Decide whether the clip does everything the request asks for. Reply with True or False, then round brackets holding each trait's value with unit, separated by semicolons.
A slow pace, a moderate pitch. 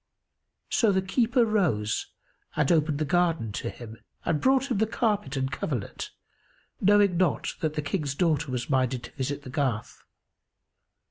False (155 wpm; 155 Hz)